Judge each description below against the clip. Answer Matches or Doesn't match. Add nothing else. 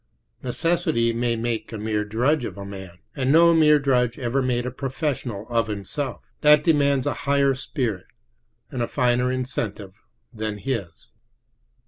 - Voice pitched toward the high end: Doesn't match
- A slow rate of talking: Doesn't match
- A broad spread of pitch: Doesn't match